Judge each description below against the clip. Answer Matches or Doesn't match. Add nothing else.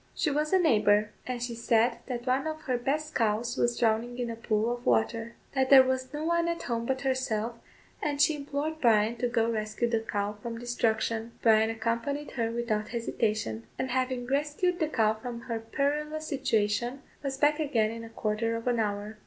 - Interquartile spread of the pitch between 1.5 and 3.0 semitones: Doesn't match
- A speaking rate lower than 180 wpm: Doesn't match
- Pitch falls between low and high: Doesn't match